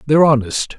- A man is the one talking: Yes, male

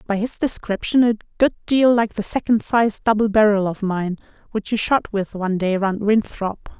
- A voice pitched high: Yes, high, 210 Hz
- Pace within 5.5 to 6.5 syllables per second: No, 5.0 syllables/s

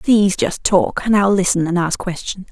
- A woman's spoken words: Yes, female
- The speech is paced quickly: No, average, 190 wpm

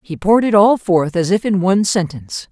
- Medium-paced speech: No, fast, 240 wpm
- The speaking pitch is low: No, high, 190 Hz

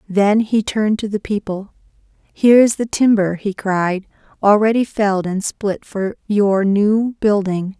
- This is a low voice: No, high, 205 Hz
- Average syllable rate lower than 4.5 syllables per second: Yes, 4.3 syllables/s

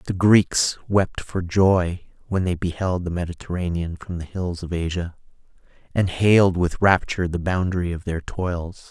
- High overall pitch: No, very low, 90 Hz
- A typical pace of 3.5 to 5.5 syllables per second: Yes, 4.6 syllables/s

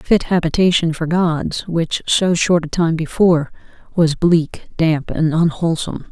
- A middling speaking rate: Yes, average, 145 wpm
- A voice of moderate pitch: Yes, medium, 165 Hz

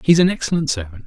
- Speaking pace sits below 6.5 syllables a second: No, 7.2 syllables/s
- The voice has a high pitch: No, medium, 140 Hz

